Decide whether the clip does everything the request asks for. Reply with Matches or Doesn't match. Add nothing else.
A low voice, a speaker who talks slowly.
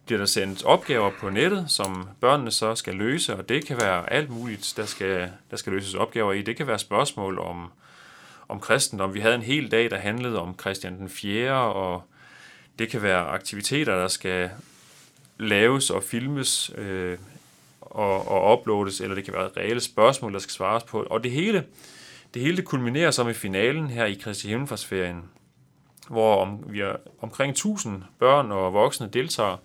Doesn't match